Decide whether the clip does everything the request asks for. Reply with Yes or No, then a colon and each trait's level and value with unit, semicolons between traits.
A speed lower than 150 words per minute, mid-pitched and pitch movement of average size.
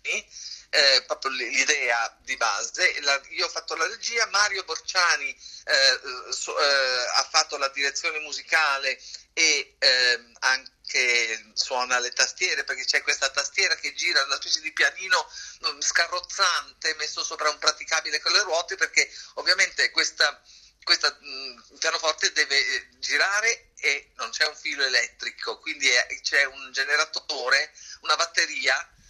Yes: average, 135 wpm; medium, 155 Hz; average, 3.4 semitones